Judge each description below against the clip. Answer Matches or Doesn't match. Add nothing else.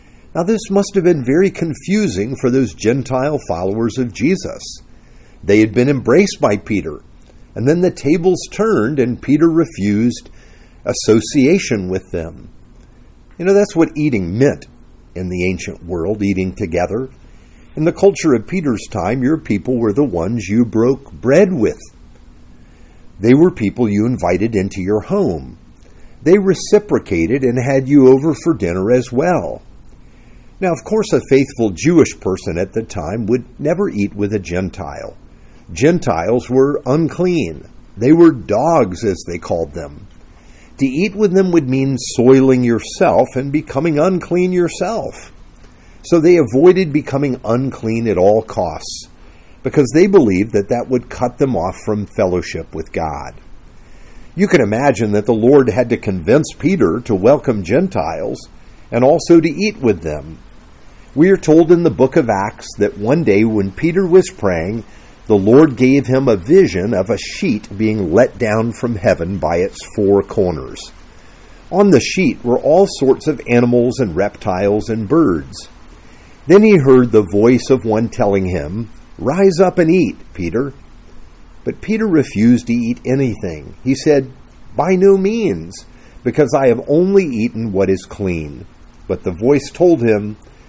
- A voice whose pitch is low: Matches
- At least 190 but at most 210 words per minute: Doesn't match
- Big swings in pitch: Matches